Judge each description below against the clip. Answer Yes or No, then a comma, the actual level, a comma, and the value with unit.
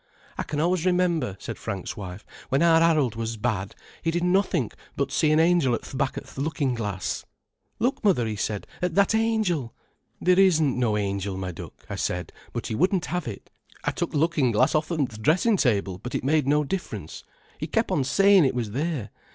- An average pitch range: No, wide, 7.6 semitones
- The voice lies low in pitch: No, medium, 145 Hz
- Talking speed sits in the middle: No, fast, 210 wpm